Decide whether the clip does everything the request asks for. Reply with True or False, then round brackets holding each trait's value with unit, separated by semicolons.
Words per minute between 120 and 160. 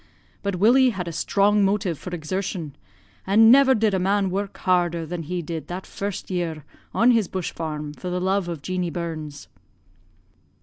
False (170 wpm)